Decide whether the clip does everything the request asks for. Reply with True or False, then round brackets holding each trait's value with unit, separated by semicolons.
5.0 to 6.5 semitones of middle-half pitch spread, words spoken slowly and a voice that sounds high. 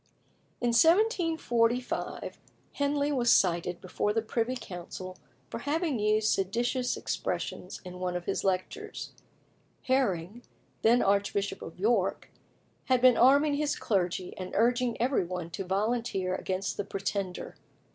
True (5.4 semitones; 125 wpm; 220 Hz)